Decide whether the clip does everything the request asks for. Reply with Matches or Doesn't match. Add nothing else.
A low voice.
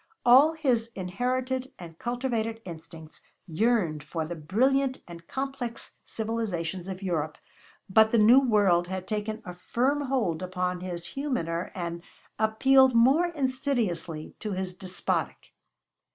Doesn't match